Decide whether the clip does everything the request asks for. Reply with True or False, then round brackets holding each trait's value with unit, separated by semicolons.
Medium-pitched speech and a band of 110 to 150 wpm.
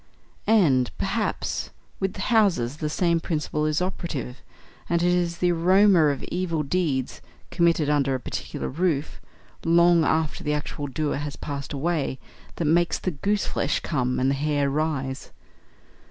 True (155 Hz; 145 wpm)